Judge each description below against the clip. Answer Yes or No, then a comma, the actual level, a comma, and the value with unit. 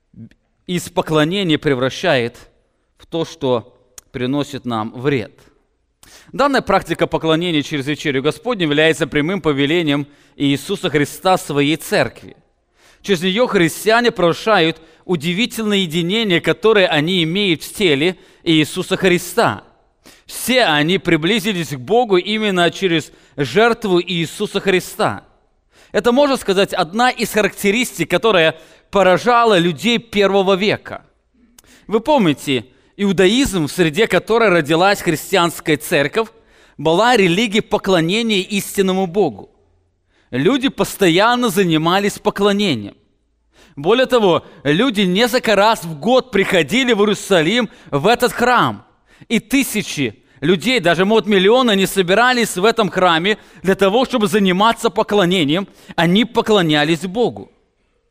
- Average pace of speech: No, slow, 110 wpm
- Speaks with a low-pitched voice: No, high, 190 Hz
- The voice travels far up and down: No, average, 5.0 semitones